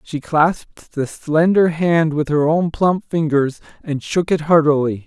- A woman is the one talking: No, male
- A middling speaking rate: Yes, average, 165 wpm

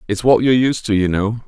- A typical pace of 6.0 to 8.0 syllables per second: Yes, 6.2 syllables/s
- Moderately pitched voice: No, low, 110 Hz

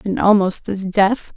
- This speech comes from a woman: Yes, female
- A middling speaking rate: Yes, average, 175 wpm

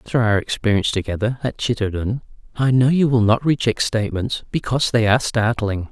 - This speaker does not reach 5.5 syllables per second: No, 6.0 syllables/s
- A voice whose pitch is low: Yes, low, 115 Hz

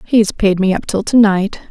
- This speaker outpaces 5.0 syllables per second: No, 4.6 syllables/s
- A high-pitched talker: Yes, high, 200 Hz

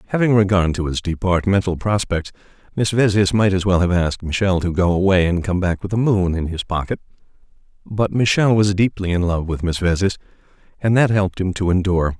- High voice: No, very low, 95 Hz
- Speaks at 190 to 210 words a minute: Yes, average, 200 wpm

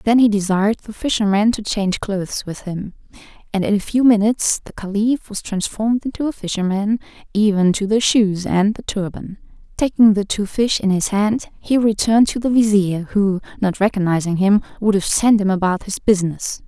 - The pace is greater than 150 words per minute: Yes, average, 185 wpm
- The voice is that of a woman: Yes, female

